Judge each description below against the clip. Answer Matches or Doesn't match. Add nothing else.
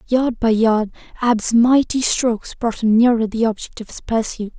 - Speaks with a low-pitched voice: Doesn't match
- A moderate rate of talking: Matches